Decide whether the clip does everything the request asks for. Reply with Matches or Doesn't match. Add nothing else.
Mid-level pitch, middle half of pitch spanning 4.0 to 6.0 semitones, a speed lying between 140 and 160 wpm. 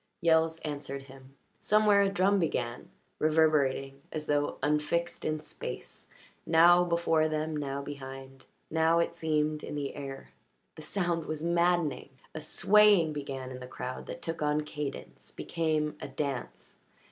Doesn't match